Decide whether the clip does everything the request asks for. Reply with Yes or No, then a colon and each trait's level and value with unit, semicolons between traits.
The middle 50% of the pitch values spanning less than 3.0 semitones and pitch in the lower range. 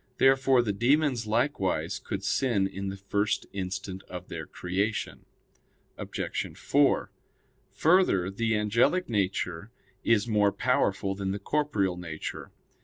No: average, 3.8 semitones; low, 105 Hz